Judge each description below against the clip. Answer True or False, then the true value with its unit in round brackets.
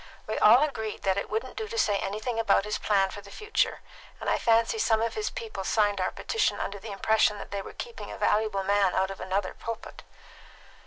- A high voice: True (215 Hz)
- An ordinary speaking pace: False (220 wpm)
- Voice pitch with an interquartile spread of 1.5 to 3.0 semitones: True (2.6 semitones)